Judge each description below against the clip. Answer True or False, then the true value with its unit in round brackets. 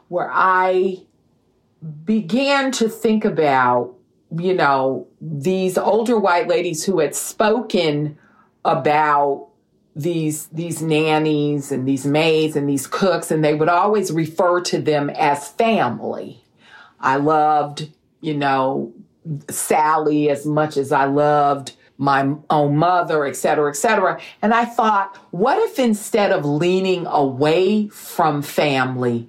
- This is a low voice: False (155 Hz)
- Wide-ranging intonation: False (4.5 semitones)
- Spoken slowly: True (125 wpm)